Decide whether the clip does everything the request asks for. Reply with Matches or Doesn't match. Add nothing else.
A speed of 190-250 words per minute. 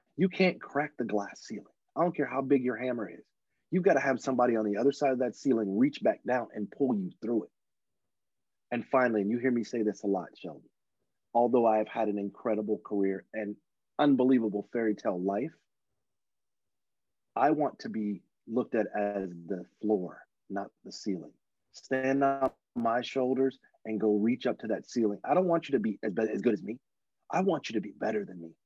Matches